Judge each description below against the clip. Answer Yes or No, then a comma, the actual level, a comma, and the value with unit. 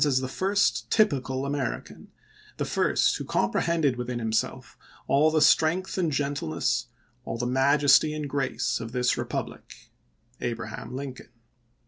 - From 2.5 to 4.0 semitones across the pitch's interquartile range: Yes, average, 3.6 semitones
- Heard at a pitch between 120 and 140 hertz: Yes, low, 135 Hz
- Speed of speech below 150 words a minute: Yes, average, 140 wpm